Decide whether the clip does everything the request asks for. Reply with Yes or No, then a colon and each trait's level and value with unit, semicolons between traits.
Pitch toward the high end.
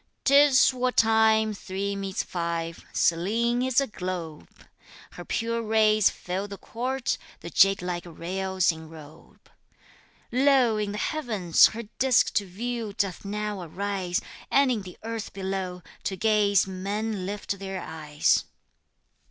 Yes: high, 200 Hz